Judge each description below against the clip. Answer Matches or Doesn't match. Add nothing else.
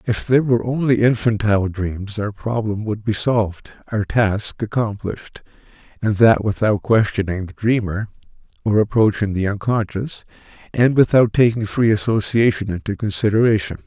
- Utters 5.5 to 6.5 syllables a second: Doesn't match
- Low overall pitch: Matches